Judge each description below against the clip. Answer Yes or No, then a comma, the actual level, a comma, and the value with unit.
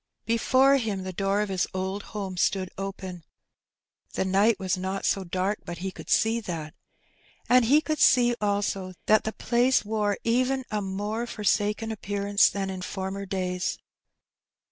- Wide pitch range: No, average, 2.9 semitones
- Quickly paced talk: No, average, 165 wpm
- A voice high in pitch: Yes, high, 200 Hz